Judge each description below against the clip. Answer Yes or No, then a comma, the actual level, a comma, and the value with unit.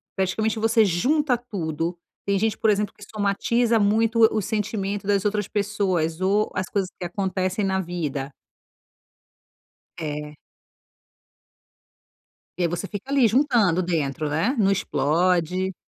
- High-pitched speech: Yes, high, 195 Hz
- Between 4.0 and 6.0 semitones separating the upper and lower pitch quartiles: No, average, 3.6 semitones